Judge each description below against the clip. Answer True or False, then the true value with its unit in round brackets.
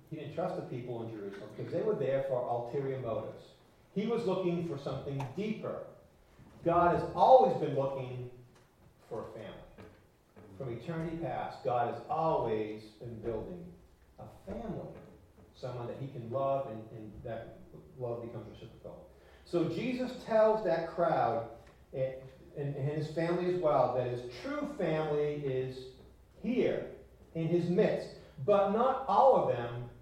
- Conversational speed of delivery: True (150 wpm)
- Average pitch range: False (6.0 semitones)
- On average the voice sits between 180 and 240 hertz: False (140 Hz)